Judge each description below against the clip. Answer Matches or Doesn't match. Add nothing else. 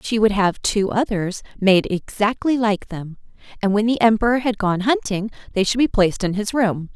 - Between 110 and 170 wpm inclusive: Doesn't match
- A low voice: Doesn't match